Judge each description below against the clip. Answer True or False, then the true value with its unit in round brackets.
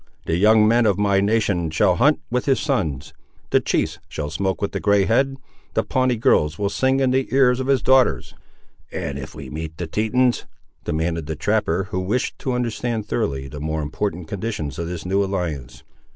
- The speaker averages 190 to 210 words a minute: True (195 wpm)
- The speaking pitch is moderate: False (100 Hz)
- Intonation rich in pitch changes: True (7.0 semitones)